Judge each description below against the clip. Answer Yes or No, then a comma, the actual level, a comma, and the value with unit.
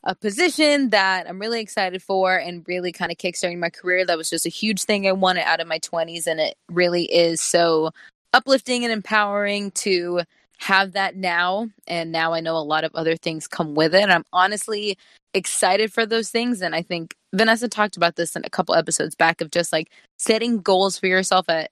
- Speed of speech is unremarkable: No, fast, 215 wpm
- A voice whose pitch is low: No, medium, 185 Hz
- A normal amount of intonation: Yes, average, 3.8 semitones